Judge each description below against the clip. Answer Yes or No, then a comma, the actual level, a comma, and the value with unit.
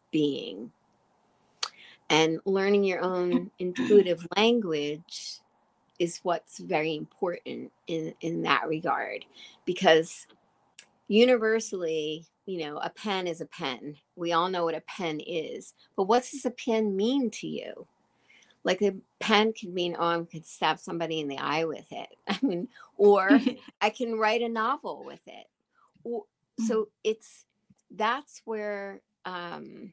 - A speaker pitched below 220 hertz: Yes, high, 190 Hz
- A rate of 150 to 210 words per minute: No, average, 140 wpm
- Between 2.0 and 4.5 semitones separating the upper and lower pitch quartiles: No, average, 5.1 semitones